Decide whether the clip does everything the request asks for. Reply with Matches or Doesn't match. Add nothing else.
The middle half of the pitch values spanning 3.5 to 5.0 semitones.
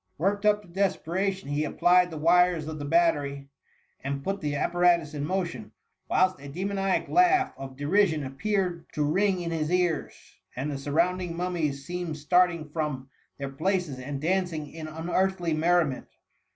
Matches